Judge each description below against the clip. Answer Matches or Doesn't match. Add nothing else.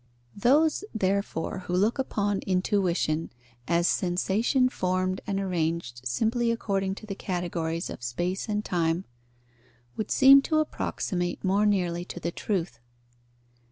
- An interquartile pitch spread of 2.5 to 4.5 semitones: Matches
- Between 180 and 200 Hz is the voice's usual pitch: Matches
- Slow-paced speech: Matches